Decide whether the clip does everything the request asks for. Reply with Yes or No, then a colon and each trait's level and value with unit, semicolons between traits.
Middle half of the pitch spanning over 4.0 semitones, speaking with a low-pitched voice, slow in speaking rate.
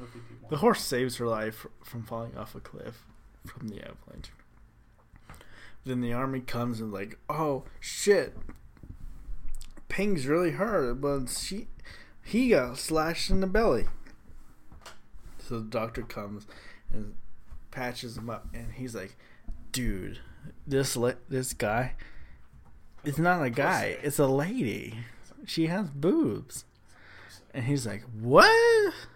Yes: average, 4.8 semitones; low, 125 Hz; slow, 130 wpm